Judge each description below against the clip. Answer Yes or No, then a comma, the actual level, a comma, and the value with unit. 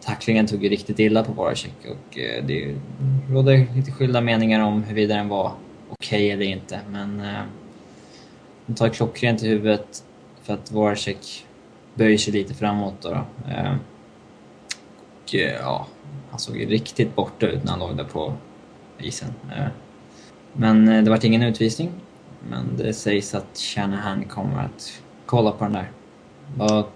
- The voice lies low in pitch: Yes, low, 105 Hz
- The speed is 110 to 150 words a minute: No, average, 160 wpm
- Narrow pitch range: Yes, narrow, 2.0 semitones